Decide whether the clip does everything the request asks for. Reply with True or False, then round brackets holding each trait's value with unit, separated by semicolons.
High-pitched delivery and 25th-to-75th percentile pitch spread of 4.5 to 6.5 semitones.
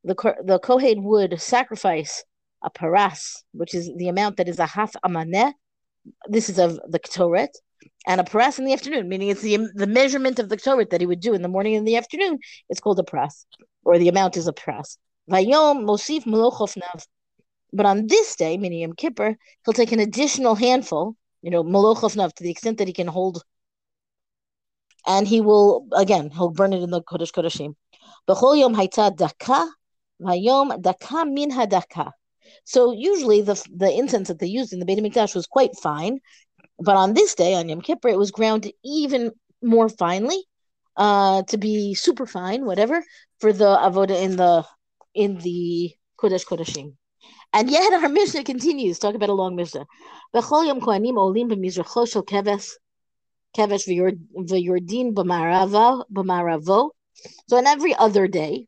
True (205 Hz; 5.2 semitones)